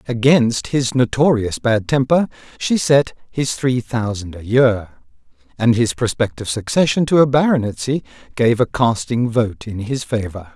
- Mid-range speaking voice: No, low, 120 Hz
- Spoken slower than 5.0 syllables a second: Yes, 4.5 syllables/s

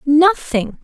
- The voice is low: No, very high, 305 Hz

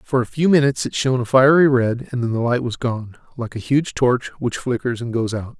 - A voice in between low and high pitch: No, low, 125 Hz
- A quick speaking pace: Yes, fast, 255 wpm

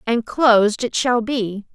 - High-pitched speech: Yes, high, 230 Hz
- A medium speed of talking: Yes, average, 170 wpm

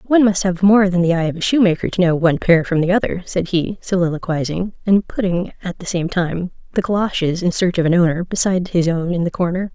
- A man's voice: No, female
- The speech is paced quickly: Yes, fast, 240 wpm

